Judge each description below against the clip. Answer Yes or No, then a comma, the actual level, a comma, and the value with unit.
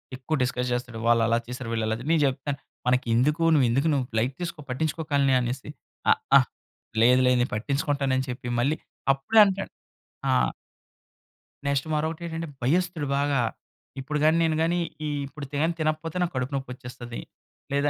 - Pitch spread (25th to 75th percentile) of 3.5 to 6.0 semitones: Yes, average, 3.9 semitones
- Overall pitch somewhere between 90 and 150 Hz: Yes, medium, 140 Hz